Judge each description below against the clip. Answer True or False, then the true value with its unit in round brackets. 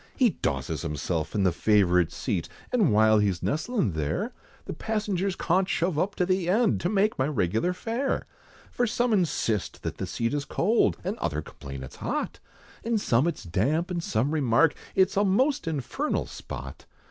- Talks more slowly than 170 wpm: False (175 wpm)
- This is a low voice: False (165 Hz)